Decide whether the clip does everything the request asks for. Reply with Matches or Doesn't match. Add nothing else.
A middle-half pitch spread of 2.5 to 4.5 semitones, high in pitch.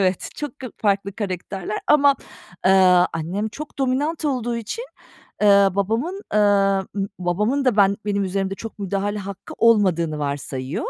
Matches